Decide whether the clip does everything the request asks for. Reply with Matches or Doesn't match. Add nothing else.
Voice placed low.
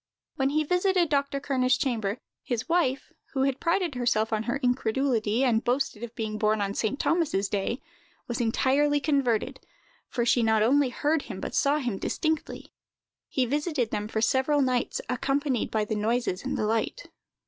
Doesn't match